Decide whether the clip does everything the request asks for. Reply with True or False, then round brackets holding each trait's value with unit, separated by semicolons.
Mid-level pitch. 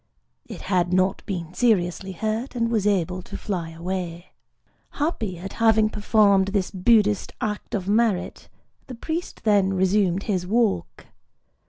False (200 Hz)